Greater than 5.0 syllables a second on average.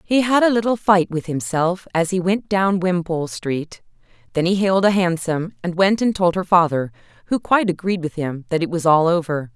Yes: 5.3 syllables/s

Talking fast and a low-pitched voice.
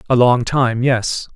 No: slow, 135 wpm; low, 125 Hz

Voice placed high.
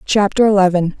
Yes: high, 195 Hz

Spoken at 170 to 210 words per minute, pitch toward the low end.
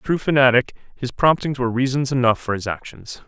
Yes: average, 200 wpm; low, 130 Hz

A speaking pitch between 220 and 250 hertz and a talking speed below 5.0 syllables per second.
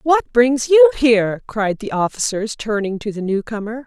Yes: high, 235 Hz; 4.6 syllables/s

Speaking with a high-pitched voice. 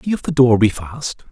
No: low, 130 Hz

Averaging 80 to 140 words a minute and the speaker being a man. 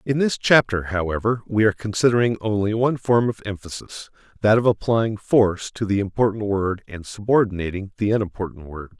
No: average, 165 wpm; male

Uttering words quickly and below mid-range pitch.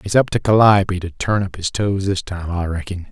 Yes: fast, 250 wpm; very low, 95 Hz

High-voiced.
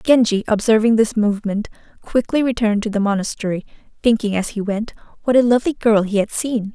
Yes: high, 220 Hz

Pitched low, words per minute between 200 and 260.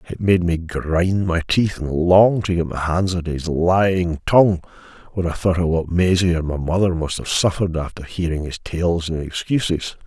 Yes: very low, 85 Hz; fast, 205 wpm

